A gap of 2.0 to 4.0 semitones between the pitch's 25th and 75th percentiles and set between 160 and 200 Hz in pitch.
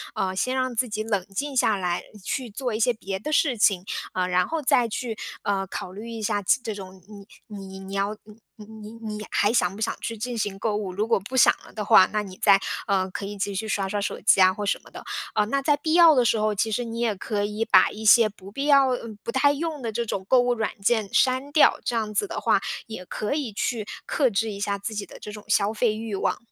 No: average, 3.2 semitones; high, 215 Hz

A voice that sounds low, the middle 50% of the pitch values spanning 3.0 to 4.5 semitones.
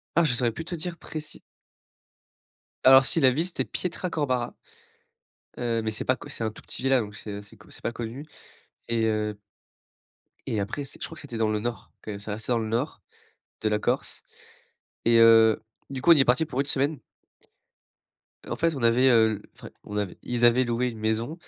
Yes: low, 120 Hz; average, 3.7 semitones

